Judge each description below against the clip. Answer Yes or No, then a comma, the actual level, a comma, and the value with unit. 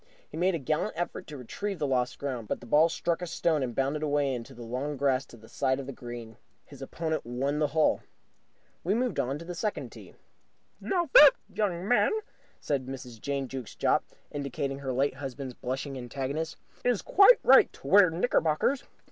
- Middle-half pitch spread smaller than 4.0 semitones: No, average, 4.4 semitones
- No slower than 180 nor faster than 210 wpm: Yes, average, 190 wpm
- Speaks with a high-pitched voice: No, medium, 140 Hz